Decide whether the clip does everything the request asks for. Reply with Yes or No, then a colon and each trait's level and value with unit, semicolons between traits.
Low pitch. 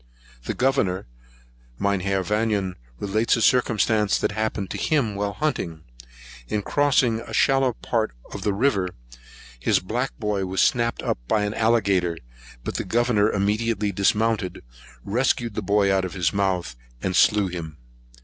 Yes: low, 105 Hz